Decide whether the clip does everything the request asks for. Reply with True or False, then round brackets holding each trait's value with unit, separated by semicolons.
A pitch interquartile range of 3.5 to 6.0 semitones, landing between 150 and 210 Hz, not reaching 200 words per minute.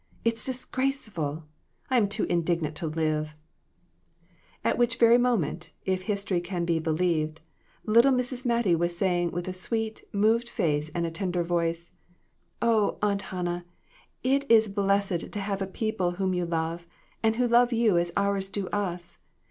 True (4.6 semitones; 190 Hz; 155 wpm)